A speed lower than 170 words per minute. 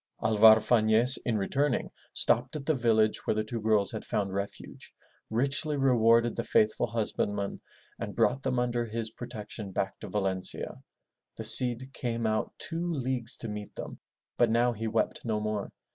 No: average, 175 wpm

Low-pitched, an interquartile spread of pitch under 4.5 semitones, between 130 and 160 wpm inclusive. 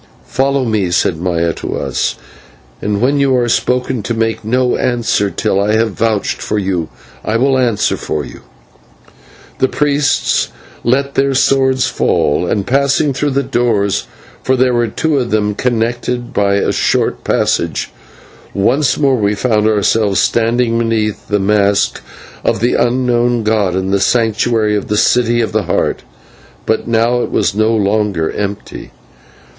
Yes: low, 115 Hz; average, 3.5 semitones; average, 155 wpm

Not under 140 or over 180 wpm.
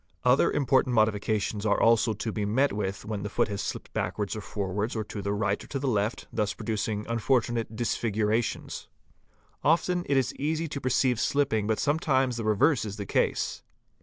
No: average, 195 wpm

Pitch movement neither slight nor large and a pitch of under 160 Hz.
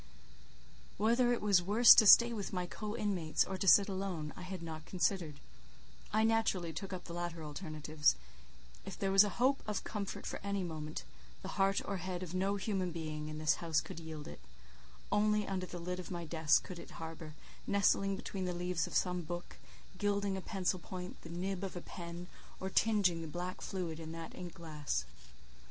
No: average, 3.1 semitones; medium, 180 Hz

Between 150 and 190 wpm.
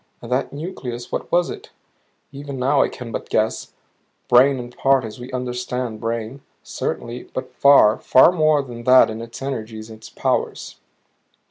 Yes: average, 160 wpm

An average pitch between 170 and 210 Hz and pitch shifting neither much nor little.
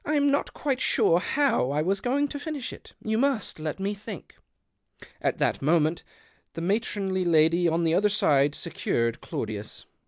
No: high, 190 Hz; wide, 7.5 semitones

